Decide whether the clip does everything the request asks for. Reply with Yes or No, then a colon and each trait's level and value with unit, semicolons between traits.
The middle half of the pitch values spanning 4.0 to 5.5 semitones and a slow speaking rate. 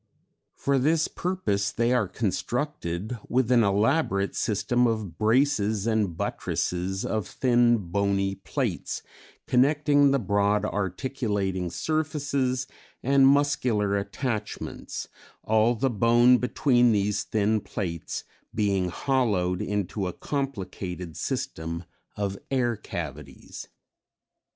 Yes: average, 4.8 semitones; slow, 105 wpm